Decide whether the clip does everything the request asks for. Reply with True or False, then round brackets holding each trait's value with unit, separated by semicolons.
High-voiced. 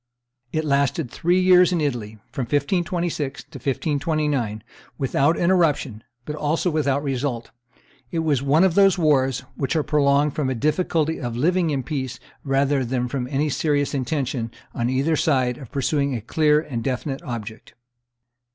False (145 Hz)